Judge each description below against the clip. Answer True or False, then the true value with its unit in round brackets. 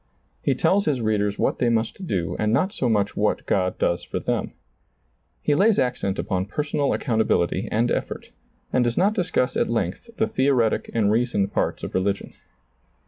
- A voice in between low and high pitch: False (115 Hz)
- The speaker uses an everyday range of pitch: False (5.7 semitones)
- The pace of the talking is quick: False (175 wpm)